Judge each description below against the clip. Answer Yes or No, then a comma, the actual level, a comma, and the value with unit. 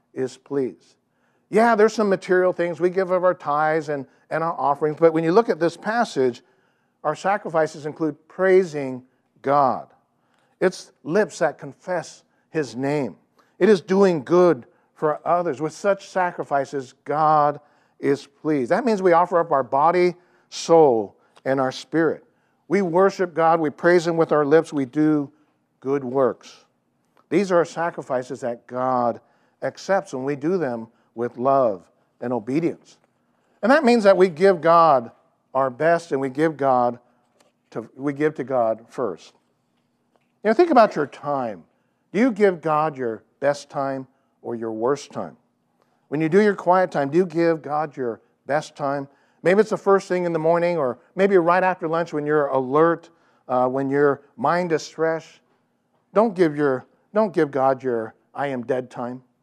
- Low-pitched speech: No, medium, 155 Hz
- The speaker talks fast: No, average, 170 wpm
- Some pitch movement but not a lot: Yes, average, 4.7 semitones